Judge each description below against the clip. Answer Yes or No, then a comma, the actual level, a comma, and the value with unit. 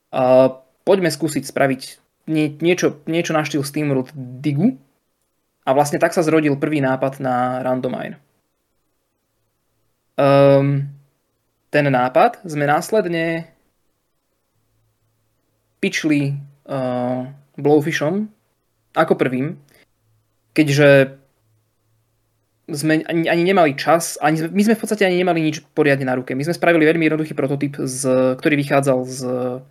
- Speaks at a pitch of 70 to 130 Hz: No, medium, 140 Hz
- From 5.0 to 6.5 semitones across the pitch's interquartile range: No, average, 3.7 semitones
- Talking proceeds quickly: No, average, 115 wpm